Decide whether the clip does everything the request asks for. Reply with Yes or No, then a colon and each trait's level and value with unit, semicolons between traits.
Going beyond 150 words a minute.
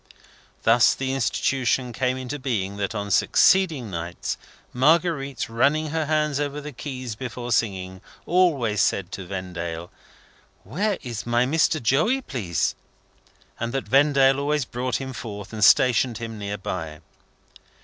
No: average, 140 wpm